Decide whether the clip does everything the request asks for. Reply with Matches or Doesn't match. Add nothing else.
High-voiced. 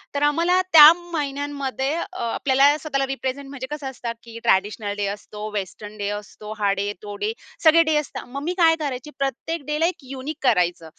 Matches